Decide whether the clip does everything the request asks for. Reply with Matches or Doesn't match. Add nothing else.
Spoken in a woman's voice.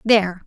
Matches